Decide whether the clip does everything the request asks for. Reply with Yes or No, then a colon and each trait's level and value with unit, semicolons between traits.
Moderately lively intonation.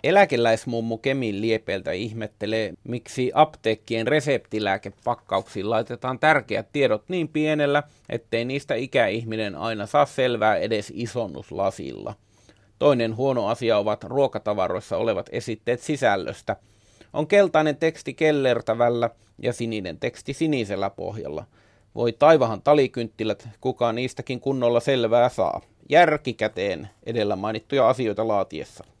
Yes: average, 3.9 semitones